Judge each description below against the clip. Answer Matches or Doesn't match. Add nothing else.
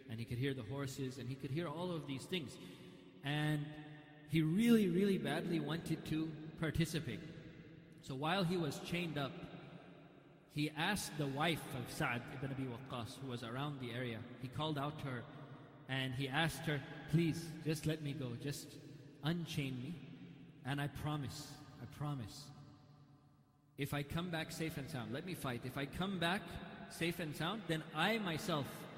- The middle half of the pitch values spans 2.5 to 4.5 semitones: Matches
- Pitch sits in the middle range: Matches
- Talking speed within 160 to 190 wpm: Matches